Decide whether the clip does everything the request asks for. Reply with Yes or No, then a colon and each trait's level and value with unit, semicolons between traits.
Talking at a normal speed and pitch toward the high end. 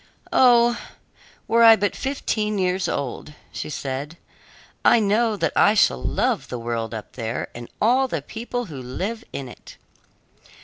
Yes: average, 150 wpm; high, 200 Hz